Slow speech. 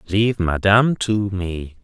Yes: slow, 130 wpm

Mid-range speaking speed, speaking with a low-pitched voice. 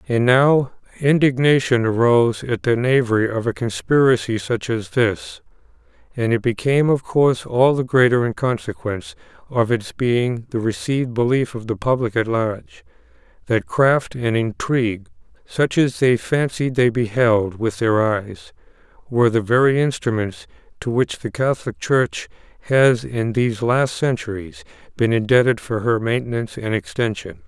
Yes: average, 145 wpm; low, 120 Hz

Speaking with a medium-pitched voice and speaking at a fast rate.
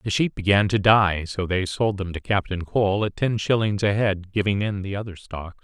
No: low, 100 Hz; fast, 235 wpm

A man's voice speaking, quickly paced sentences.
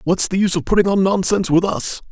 Yes: male; fast, 255 wpm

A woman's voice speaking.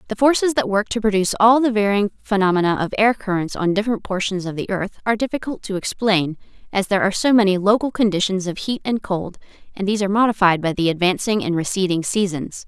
Yes: female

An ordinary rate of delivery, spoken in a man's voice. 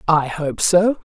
No: average, 160 wpm; female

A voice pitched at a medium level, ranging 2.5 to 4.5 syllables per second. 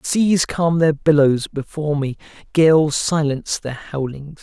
Yes: medium, 150 Hz; 4.0 syllables/s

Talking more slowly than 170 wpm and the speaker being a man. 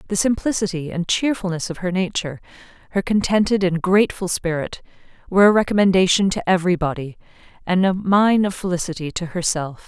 No: average, 150 wpm; female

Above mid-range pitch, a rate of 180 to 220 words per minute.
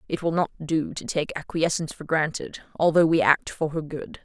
No: medium, 160 Hz; average, 200 wpm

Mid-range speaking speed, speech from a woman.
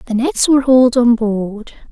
Yes: average, 190 wpm; female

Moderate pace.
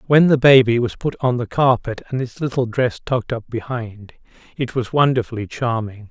Yes: average, 185 wpm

